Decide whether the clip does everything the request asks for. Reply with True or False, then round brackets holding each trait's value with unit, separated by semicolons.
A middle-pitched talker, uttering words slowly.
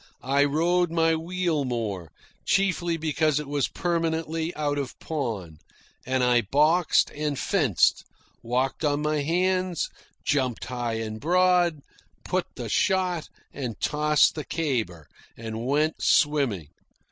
True (150 Hz; 125 wpm)